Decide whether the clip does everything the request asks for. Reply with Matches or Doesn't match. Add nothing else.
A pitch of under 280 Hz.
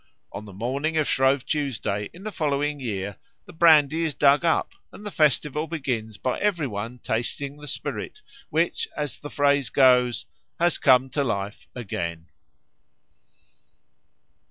Matches